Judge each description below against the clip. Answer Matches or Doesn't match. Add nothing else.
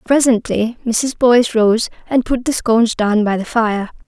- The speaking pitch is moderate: Doesn't match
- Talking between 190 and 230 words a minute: Doesn't match